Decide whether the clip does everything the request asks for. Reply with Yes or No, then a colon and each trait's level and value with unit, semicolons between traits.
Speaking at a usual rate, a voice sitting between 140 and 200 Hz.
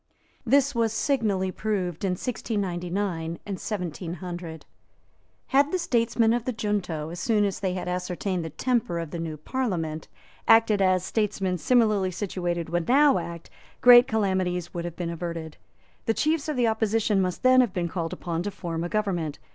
Yes: average, 170 wpm; high, 190 Hz